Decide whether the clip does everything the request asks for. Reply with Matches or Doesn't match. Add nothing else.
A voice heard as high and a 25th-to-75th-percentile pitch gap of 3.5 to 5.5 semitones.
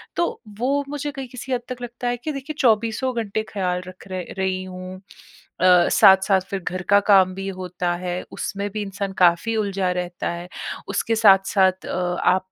Matches